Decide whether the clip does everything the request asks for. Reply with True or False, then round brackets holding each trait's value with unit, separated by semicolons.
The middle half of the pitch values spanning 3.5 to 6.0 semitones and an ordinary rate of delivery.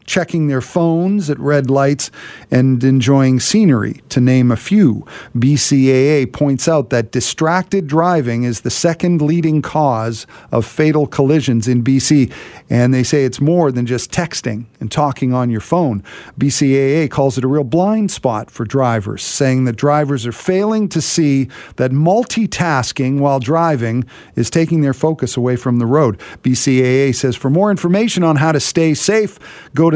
True (4.2 semitones; 165 wpm)